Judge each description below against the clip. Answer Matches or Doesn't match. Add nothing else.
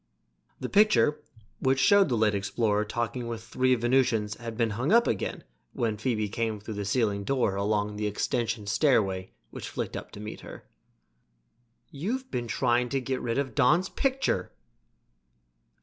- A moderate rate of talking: Matches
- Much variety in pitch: Doesn't match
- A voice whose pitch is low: Matches